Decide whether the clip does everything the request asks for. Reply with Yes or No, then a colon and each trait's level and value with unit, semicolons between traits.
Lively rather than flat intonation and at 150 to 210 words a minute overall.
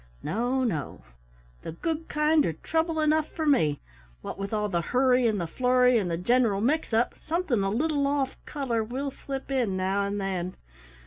Yes: wide, 6.4 semitones; average, 180 wpm